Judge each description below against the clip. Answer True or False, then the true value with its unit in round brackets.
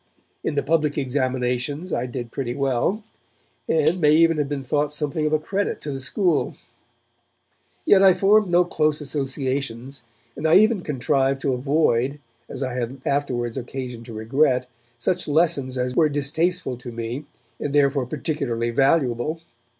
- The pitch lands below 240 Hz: True (140 Hz)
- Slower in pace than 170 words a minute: True (155 wpm)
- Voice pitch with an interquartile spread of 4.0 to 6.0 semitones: False (3.5 semitones)